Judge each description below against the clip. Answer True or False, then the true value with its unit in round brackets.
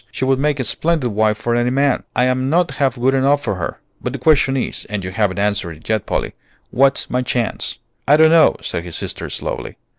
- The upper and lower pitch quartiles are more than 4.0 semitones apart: True (4.4 semitones)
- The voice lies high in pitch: False (130 Hz)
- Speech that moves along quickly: True (220 wpm)